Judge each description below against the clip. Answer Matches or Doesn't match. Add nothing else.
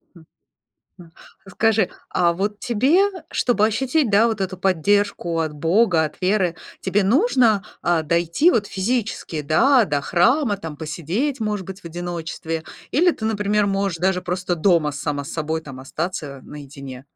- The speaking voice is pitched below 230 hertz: Matches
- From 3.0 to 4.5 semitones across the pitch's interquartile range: Doesn't match